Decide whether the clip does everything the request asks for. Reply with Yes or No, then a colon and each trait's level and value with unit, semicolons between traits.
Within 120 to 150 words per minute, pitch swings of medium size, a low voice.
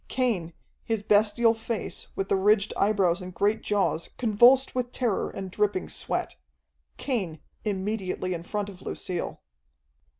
No: slow, 135 wpm; average, 3.1 semitones; high, 205 Hz